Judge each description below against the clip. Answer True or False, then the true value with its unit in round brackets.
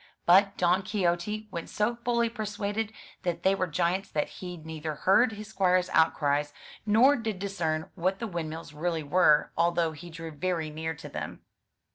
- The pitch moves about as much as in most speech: True (4.2 semitones)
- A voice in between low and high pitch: True (180 Hz)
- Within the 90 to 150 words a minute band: False (165 wpm)